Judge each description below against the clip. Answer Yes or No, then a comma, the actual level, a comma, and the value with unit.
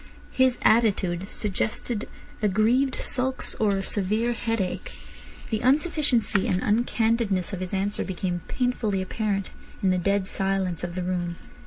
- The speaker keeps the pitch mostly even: No, average, 3.7 semitones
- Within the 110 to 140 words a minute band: Yes, slow, 135 wpm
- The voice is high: Yes, high, 205 Hz